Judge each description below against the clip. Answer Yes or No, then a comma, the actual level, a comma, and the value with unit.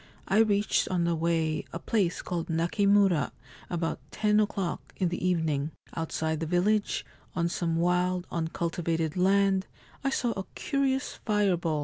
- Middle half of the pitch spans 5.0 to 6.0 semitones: No, average, 3.3 semitones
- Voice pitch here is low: No, medium, 175 Hz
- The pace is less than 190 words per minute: Yes, average, 140 wpm